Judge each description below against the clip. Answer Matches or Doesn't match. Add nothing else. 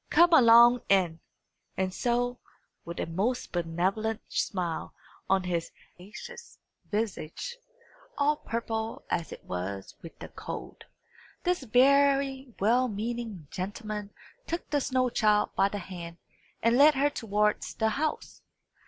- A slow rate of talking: Matches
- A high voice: Matches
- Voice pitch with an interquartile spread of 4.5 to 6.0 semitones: Matches